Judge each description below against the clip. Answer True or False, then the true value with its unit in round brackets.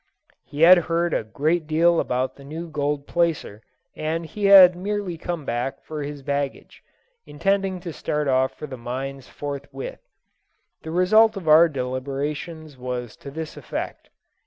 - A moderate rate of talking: True (155 wpm)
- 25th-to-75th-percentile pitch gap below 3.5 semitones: False (3.9 semitones)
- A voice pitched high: False (155 Hz)